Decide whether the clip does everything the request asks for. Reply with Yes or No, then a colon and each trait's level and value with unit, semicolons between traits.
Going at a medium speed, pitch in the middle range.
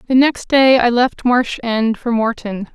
No: average, 195 wpm; high, 240 Hz